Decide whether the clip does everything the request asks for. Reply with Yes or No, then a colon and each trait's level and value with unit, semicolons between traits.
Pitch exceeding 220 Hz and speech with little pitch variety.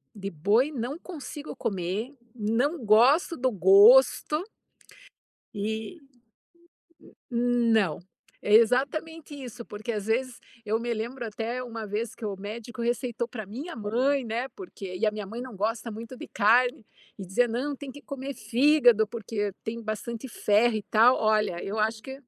No: high, 235 Hz; average, 3.3 semitones